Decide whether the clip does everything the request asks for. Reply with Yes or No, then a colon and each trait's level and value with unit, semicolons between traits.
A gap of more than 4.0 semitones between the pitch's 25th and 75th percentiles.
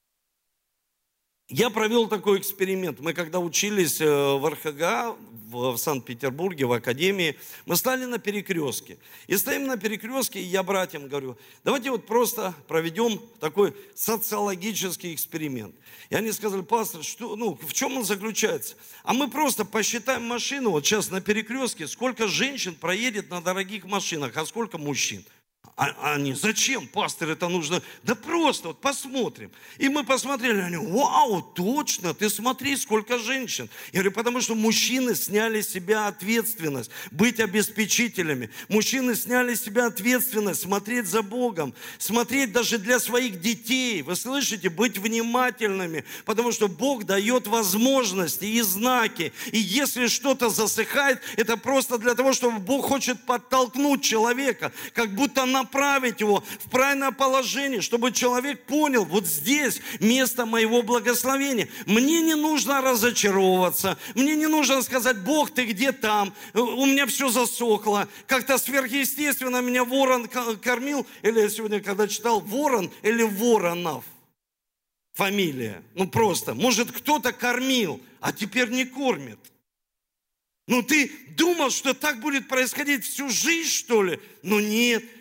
Yes: average, 4.6 semitones